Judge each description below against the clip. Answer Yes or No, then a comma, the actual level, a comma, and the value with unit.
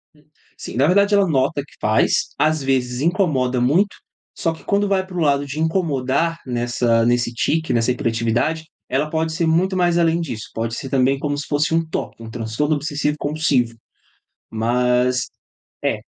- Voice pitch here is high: No, medium, 145 Hz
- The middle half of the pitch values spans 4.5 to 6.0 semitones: Yes, average, 4.8 semitones